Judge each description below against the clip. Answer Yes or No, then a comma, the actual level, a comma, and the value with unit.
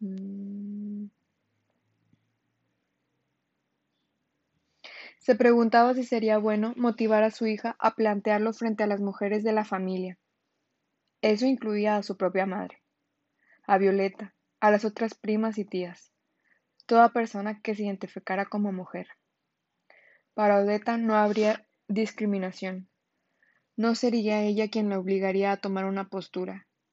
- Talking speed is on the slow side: Yes, slow, 120 wpm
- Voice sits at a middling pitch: No, high, 210 Hz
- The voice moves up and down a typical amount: No, narrow, 2.0 semitones